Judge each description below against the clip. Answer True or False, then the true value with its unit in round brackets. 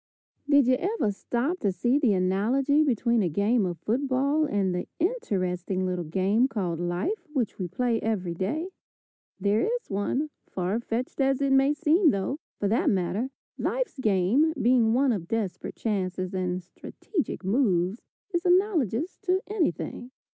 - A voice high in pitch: True (230 Hz)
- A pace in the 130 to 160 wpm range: True (155 wpm)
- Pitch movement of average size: False (7.1 semitones)